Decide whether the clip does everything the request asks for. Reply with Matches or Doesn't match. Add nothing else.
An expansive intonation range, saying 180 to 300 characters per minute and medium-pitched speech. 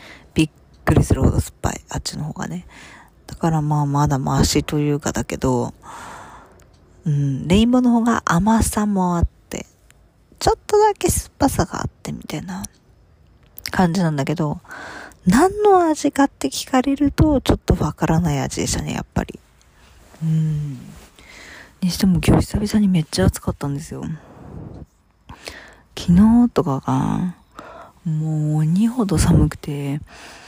Matches